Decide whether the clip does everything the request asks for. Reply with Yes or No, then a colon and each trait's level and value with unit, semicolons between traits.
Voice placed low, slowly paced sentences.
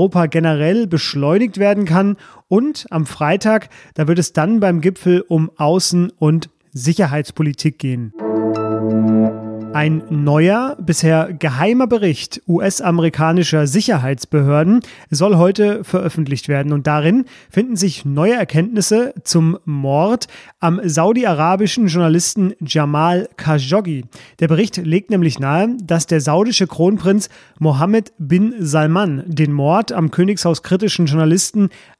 No: medium, 170 Hz; slow, 115 wpm